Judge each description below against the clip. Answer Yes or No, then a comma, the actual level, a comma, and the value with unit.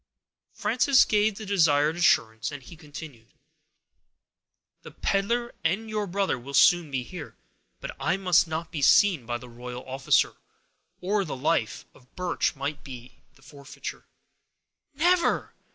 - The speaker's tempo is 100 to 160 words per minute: Yes, average, 140 wpm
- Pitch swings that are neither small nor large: No, wide, 6.8 semitones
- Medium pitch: Yes, medium, 160 Hz